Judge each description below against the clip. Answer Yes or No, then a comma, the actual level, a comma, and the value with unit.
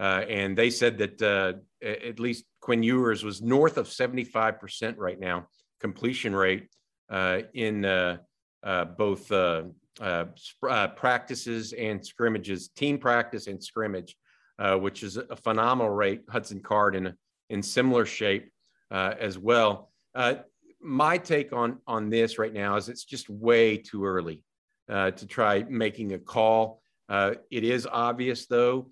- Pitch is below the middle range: Yes, low, 110 Hz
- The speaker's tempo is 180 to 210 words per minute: No, average, 150 wpm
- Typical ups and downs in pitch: Yes, average, 3.4 semitones